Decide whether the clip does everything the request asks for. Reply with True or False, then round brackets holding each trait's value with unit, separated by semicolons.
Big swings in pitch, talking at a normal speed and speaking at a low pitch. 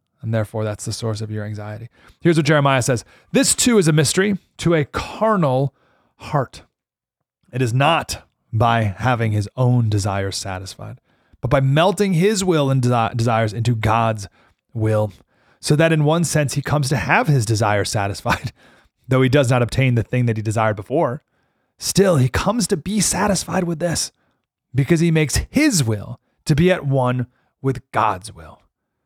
True (6.4 semitones; 170 wpm; 125 Hz)